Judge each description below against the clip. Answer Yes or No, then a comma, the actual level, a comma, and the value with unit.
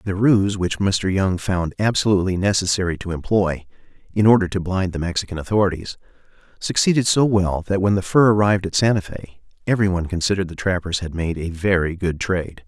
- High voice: No, very low, 95 Hz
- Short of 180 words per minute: No, average, 185 wpm